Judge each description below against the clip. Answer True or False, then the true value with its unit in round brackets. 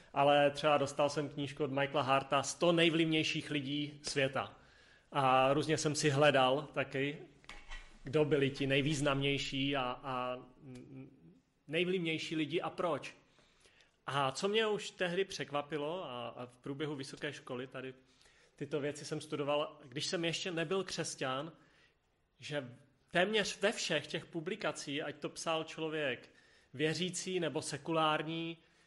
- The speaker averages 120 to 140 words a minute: True (130 wpm)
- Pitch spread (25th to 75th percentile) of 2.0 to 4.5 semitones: True (2.8 semitones)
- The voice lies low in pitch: False (150 Hz)